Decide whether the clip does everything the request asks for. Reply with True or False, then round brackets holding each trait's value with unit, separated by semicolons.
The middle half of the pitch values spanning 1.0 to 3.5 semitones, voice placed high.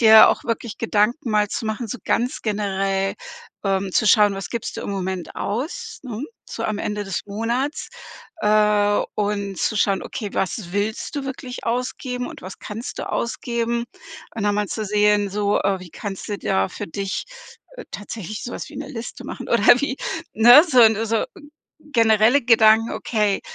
True (2.8 semitones; 215 Hz)